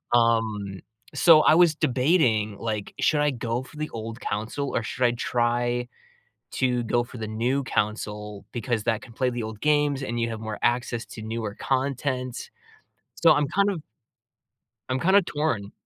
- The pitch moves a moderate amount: Yes, average, 3.6 semitones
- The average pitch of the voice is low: Yes, low, 120 Hz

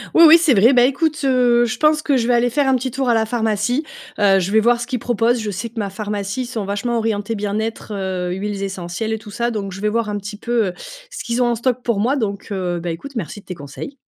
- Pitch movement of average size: Yes, average, 3.4 semitones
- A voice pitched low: No, high, 225 Hz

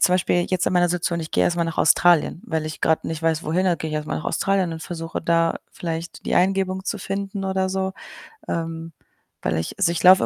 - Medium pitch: Yes, medium, 170 Hz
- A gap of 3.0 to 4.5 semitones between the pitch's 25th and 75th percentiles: No, narrow, 2.4 semitones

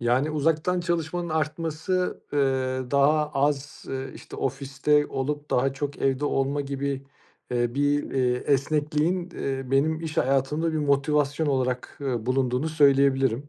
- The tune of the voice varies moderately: No, narrow, 2.3 semitones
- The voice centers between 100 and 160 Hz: Yes, medium, 140 Hz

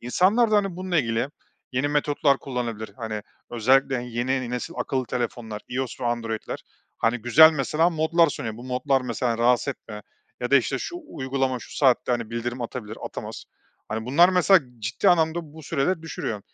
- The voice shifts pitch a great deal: No, average, 4.8 semitones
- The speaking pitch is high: No, low, 130 Hz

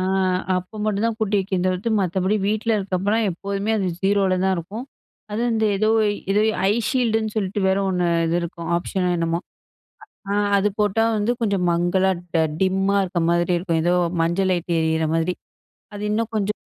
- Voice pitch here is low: No, high, 190 Hz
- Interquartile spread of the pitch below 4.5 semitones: Yes, average, 2.9 semitones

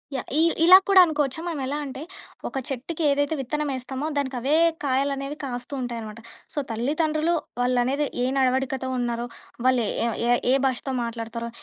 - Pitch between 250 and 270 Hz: Yes, very high, 265 Hz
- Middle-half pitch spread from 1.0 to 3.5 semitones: Yes, average, 2.8 semitones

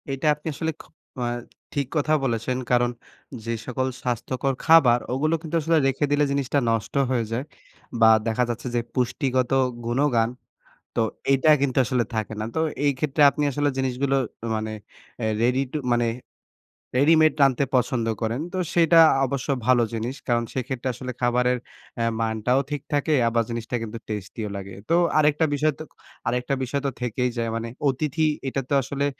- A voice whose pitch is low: Yes, low, 130 Hz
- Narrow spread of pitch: No, average, 3.2 semitones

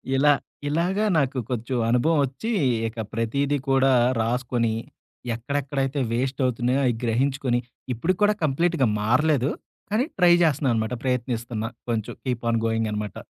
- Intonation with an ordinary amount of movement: Yes, average, 3.6 semitones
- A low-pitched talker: Yes, low, 130 Hz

